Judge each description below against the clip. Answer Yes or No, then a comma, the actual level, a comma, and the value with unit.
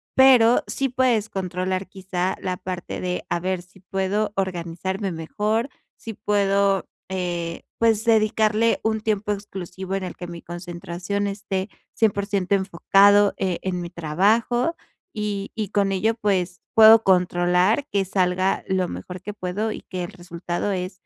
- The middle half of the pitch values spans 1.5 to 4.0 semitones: Yes, narrow, 2.6 semitones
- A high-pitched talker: Yes, high, 195 Hz